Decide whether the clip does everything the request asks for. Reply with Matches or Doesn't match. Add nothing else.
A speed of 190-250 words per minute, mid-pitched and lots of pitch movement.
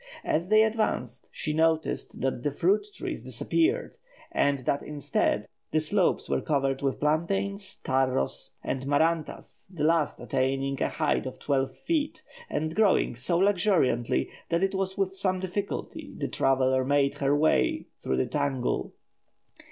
Doesn't match